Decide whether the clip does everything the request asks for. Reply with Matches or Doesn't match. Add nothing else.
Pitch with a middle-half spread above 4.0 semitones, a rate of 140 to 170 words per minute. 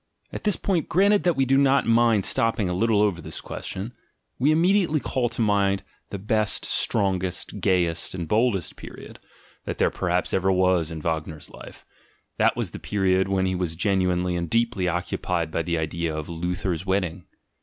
Doesn't match